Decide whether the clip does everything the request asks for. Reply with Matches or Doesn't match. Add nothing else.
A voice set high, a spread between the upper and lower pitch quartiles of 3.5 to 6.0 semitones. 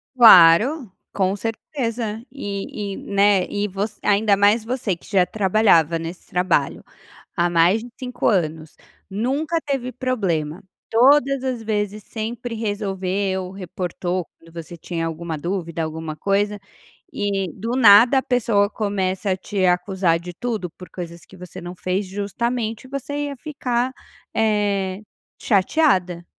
Matches